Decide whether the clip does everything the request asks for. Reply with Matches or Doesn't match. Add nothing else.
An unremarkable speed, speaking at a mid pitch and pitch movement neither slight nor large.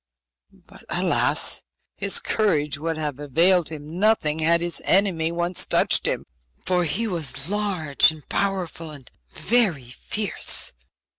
Doesn't match